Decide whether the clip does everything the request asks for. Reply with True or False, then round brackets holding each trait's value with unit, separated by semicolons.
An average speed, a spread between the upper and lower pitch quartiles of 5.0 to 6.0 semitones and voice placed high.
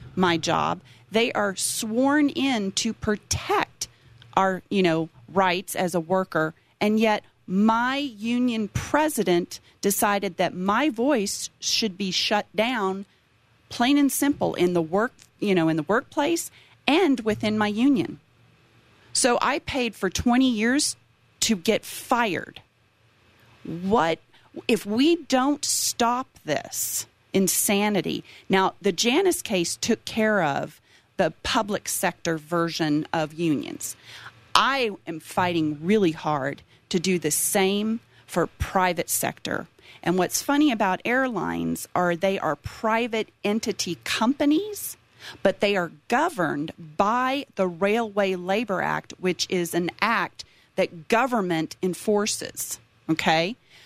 False (125 wpm; 5.3 semitones; 195 Hz)